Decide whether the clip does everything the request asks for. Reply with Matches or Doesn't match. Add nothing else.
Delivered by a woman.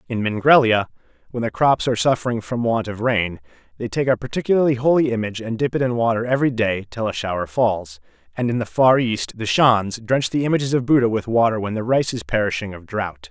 Doesn't match